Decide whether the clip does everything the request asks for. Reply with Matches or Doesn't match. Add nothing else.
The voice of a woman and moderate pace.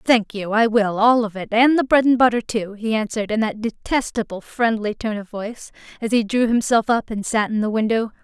Doesn't match